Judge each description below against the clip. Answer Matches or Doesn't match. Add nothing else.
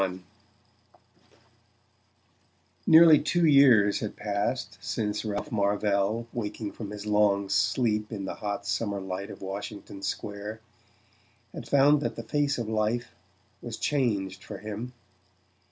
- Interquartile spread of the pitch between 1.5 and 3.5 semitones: Matches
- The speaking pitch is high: Doesn't match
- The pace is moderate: Doesn't match